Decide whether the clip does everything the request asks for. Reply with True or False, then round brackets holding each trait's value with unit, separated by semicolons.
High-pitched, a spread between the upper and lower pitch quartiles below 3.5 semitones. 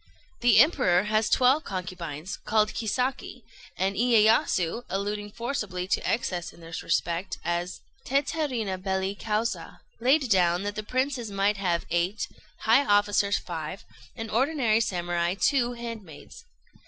False (205 Hz; 4.6 semitones)